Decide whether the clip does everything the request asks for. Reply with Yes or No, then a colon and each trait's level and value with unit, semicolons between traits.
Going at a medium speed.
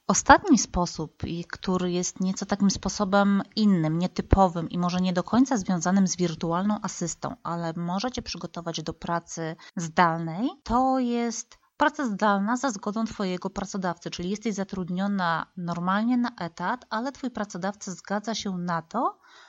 Yes: average, 140 wpm